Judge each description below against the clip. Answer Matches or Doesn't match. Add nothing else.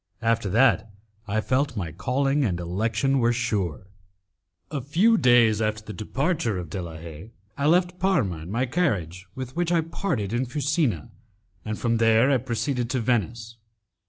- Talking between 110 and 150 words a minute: Doesn't match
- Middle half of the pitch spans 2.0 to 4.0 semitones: Doesn't match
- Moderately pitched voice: Doesn't match